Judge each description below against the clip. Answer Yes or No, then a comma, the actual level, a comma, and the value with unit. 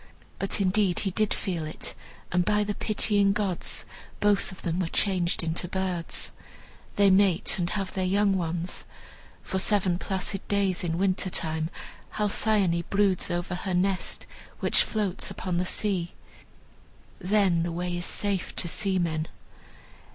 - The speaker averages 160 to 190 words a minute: No, average, 145 wpm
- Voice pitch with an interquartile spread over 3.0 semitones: No, narrow, 2.4 semitones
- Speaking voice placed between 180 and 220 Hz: Yes, medium, 185 Hz